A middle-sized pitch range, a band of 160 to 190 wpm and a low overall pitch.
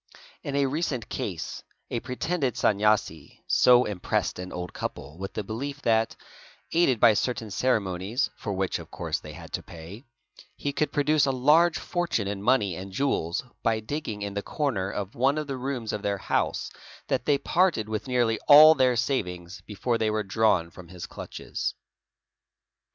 No: wide, 5.7 semitones; average, 175 wpm; low, 115 Hz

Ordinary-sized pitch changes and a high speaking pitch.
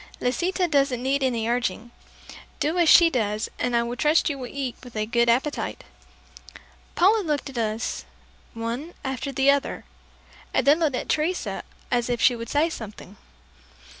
Yes: average, 4.2 semitones; very high, 260 Hz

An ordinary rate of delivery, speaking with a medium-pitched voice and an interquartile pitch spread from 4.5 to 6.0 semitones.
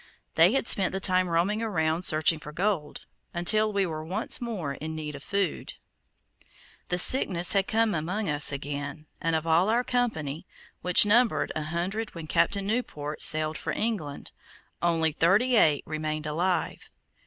Yes: average, 160 wpm; medium, 170 Hz; average, 4.8 semitones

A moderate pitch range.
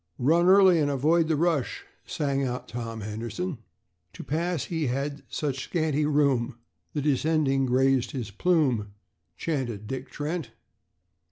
Yes: average, 4.2 semitones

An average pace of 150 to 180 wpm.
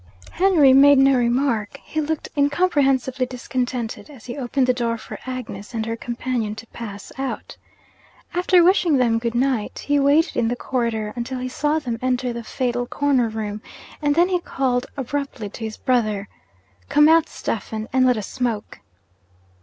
Yes: average, 170 wpm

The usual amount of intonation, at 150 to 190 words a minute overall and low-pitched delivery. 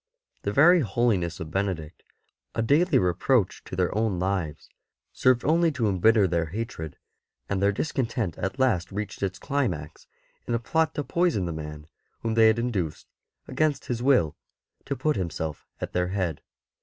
No: wide, 6.6 semitones; average, 175 wpm; low, 105 Hz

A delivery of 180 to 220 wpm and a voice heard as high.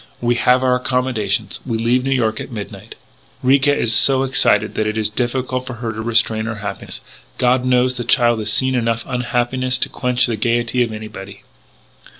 No: average, 185 wpm; low, 120 Hz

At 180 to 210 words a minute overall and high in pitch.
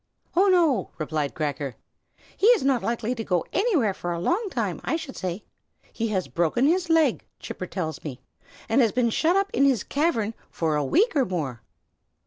Yes: average, 190 wpm; high, 230 Hz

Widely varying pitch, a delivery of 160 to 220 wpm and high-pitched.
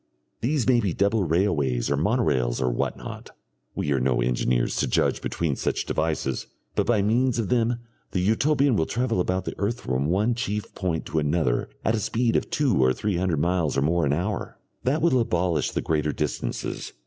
No: wide, 7.6 semitones; average, 195 wpm; very low, 90 Hz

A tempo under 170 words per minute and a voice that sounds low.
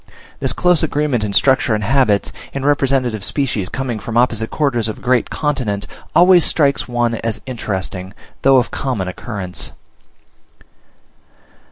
Yes: average, 140 wpm; low, 120 Hz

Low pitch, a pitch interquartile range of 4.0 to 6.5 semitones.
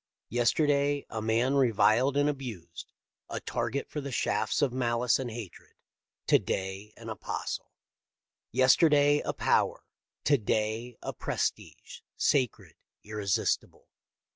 Yes: low, 120 Hz; average, 4.4 semitones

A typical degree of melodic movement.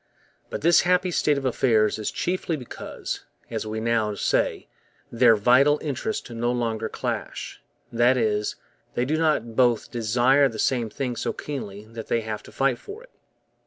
Yes: average, 4.0 semitones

